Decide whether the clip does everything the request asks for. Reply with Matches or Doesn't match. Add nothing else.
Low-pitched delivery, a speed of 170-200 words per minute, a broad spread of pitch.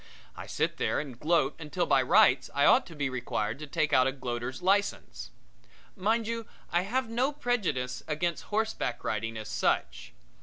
Doesn't match